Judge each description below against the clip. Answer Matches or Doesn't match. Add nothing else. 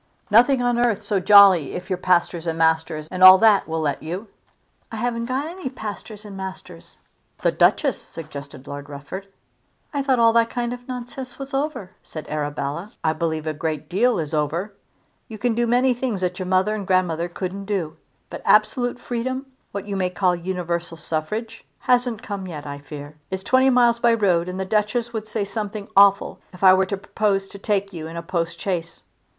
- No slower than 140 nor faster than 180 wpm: Doesn't match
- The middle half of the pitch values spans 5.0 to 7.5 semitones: Matches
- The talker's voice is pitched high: Matches